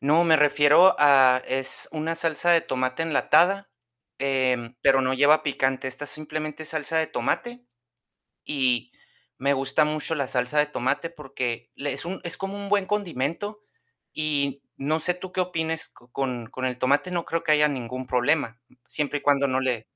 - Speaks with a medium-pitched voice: Yes, medium, 145 Hz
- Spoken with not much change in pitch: No, average, 3.7 semitones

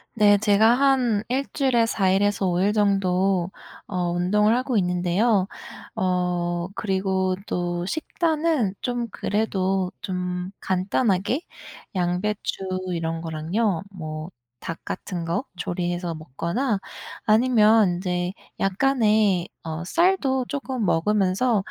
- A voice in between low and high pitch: No, high, 195 Hz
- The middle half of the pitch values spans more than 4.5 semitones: No, average, 3.8 semitones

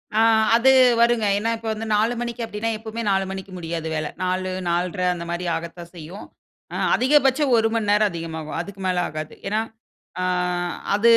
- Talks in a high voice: Yes, high, 200 Hz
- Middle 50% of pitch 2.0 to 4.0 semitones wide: No, average, 4.8 semitones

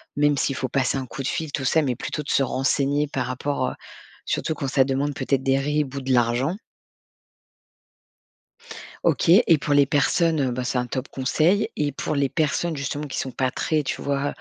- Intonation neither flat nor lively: No, narrow, 2.0 semitones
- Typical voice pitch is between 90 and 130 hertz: No, medium, 140 Hz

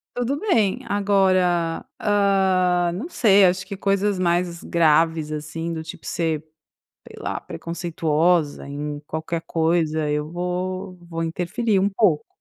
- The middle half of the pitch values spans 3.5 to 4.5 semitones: No, average, 3.1 semitones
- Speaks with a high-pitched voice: No, medium, 175 Hz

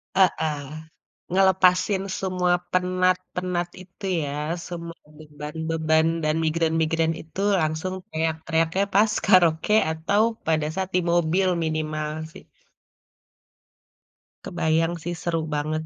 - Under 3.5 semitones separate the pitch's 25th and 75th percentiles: Yes, narrow, 2.5 semitones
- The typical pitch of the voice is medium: Yes, medium, 165 Hz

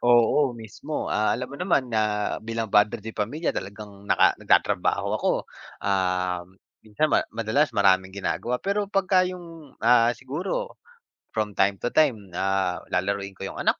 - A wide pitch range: Yes, wide, 6.3 semitones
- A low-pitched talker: Yes, low, 110 Hz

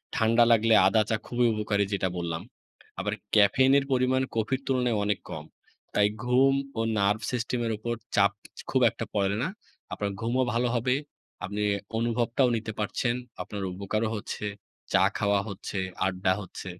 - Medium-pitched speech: No, low, 110 Hz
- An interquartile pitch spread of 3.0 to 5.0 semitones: Yes, average, 3.3 semitones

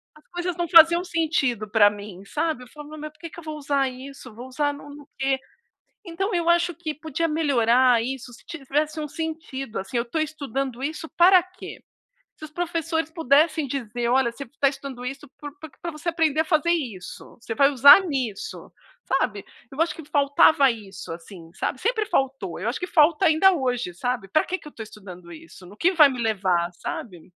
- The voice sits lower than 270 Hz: No, very high, 280 Hz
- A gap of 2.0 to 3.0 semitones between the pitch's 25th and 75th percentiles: No, average, 5.1 semitones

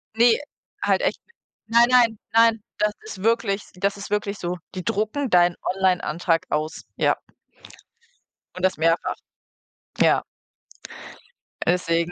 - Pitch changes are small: No, average, 4.2 semitones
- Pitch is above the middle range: Yes, high, 200 Hz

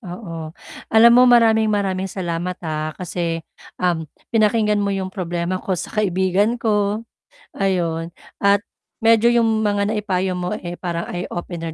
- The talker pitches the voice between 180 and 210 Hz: Yes, medium, 185 Hz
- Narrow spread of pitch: No, average, 3.3 semitones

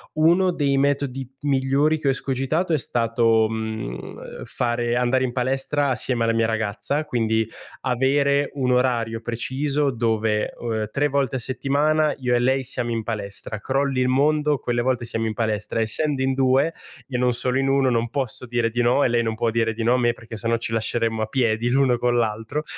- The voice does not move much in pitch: No, average, 3.1 semitones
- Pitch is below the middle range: Yes, low, 125 Hz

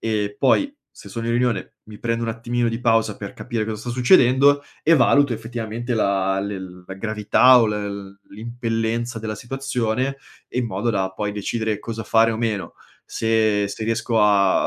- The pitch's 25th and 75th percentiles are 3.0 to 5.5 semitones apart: No, narrow, 2.4 semitones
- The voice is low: Yes, low, 115 Hz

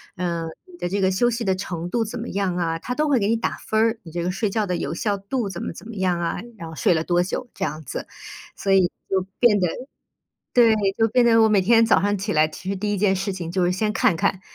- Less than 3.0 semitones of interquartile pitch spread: No, average, 4.0 semitones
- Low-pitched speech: No, high, 195 Hz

